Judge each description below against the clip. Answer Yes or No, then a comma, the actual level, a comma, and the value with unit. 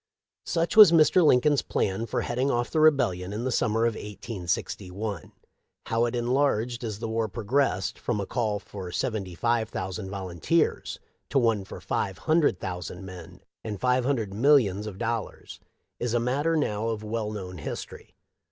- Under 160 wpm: No, average, 170 wpm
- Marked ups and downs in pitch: No, average, 4.4 semitones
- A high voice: No, low, 110 Hz